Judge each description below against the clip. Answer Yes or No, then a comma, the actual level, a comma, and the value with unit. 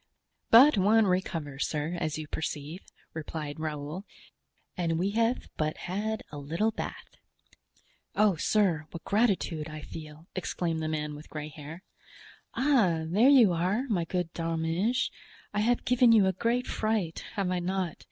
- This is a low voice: No, medium, 175 Hz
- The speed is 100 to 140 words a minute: No, average, 150 wpm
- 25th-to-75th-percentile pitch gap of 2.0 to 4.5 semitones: No, average, 5.2 semitones